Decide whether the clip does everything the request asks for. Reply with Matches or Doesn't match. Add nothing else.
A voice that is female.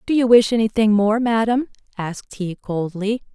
Matches